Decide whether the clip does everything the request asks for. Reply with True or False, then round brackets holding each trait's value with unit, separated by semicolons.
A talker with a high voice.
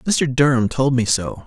False (130 Hz)